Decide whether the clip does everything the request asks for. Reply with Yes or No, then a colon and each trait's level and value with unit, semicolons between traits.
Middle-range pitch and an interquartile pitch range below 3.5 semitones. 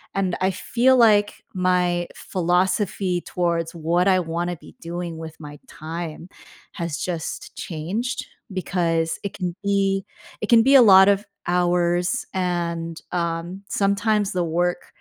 Yes: medium, 180 Hz; narrow, 2.5 semitones